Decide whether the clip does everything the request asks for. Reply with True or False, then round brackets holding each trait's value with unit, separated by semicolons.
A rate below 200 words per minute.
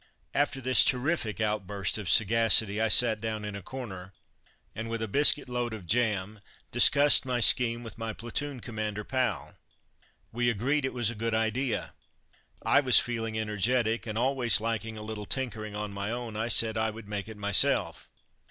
True (170 wpm)